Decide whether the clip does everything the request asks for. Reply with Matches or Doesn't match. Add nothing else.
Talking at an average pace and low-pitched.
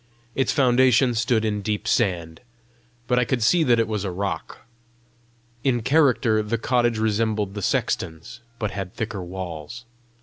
Matches